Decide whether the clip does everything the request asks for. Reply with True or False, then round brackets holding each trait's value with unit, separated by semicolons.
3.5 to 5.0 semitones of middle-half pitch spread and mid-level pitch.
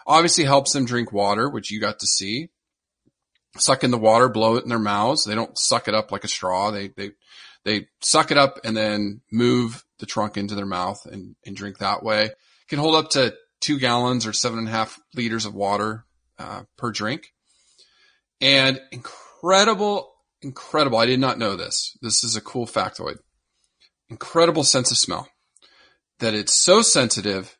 False (4.6 semitones; 115 Hz)